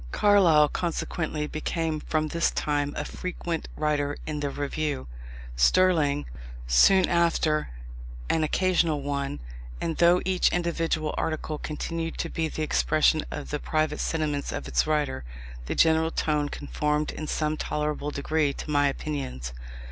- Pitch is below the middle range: No, medium, 155 Hz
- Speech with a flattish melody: Yes, narrow, 1.9 semitones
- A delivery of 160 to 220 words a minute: No, average, 140 wpm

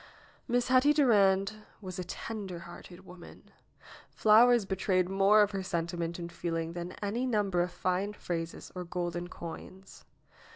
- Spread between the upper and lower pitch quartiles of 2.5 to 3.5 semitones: Yes, average, 3.2 semitones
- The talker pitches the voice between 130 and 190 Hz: Yes, medium, 185 Hz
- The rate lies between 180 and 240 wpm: No, average, 140 wpm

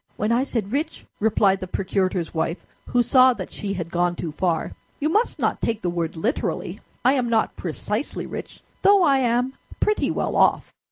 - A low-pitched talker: No, high, 215 Hz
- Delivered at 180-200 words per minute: Yes, average, 185 wpm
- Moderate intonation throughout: No, wide, 6.5 semitones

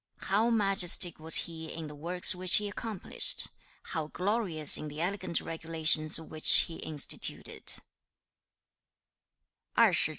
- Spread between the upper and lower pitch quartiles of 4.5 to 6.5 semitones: No, average, 3.8 semitones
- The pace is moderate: No, slow, 120 wpm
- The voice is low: No, medium, 165 Hz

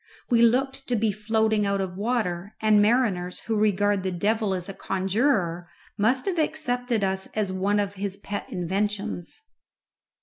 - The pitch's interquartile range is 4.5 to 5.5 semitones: No, average, 3.1 semitones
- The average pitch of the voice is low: No, high, 205 Hz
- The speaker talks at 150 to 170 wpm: Yes, average, 160 wpm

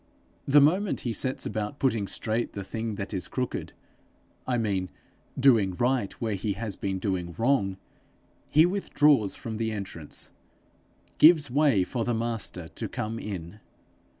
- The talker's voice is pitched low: Yes, low, 110 Hz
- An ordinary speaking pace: Yes, average, 150 wpm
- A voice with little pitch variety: No, average, 4.8 semitones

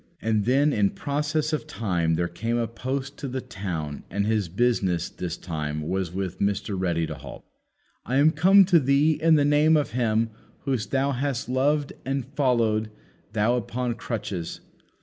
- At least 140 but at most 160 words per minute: No, average, 170 wpm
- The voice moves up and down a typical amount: No, wide, 6.3 semitones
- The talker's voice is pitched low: Yes, low, 120 Hz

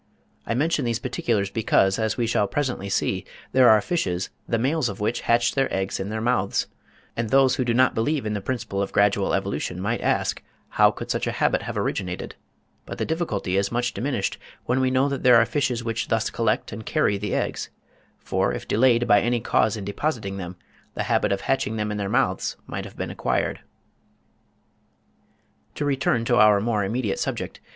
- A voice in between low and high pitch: No, low, 115 Hz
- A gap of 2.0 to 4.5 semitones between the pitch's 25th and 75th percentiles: Yes, average, 3.9 semitones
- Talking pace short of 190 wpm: No, average, 200 wpm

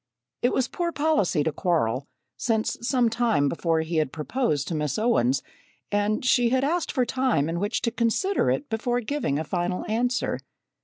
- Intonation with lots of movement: Yes, wide, 7.6 semitones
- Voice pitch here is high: Yes, high, 220 Hz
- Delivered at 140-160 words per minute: No, average, 175 wpm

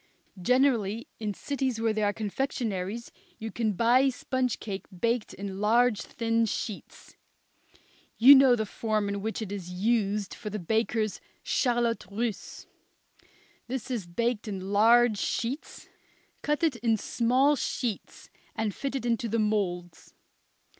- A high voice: Yes, high, 225 Hz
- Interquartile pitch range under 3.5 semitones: Yes, average, 2.9 semitones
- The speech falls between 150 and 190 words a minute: No, average, 140 wpm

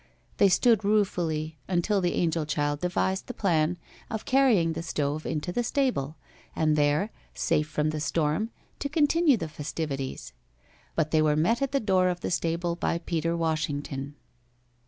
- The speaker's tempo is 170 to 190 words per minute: No, average, 160 wpm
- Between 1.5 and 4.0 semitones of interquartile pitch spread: No, average, 4.6 semitones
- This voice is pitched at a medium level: Yes, medium, 165 Hz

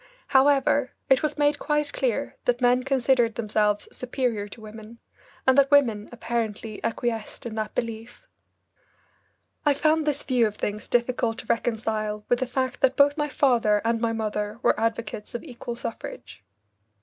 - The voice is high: Yes, high, 235 Hz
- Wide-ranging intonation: No, average, 3.5 semitones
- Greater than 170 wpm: No, average, 160 wpm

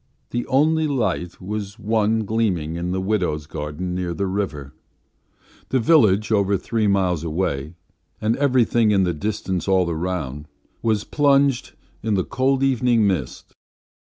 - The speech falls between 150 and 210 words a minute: No, average, 140 wpm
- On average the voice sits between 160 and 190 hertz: No, low, 100 Hz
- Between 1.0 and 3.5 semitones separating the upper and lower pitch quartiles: No, average, 4.4 semitones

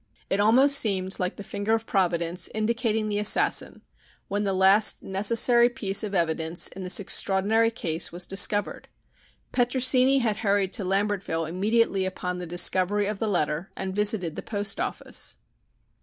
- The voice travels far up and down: No, average, 2.9 semitones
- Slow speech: No, average, 155 wpm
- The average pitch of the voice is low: No, high, 200 Hz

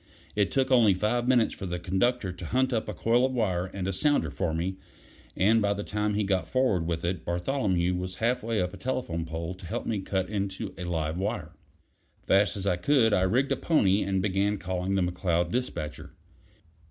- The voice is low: Yes, very low, 95 Hz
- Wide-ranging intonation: No, average, 4.1 semitones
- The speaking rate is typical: No, fast, 215 wpm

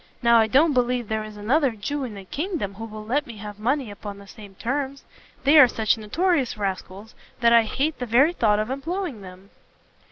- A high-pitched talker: Yes, high, 235 Hz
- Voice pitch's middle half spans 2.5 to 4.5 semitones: No, average, 4.9 semitones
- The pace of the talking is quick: Yes, fast, 210 wpm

